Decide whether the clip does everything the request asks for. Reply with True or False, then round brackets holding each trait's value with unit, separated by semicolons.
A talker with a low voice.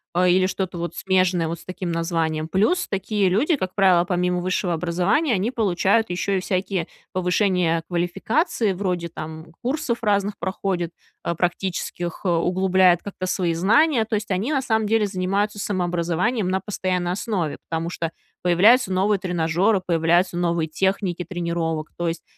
False (185 Hz)